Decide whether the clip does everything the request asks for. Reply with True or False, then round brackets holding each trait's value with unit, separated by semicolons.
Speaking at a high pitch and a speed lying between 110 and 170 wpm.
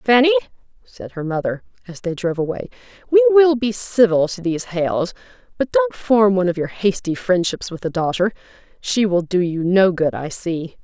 False (195 Hz; 190 wpm)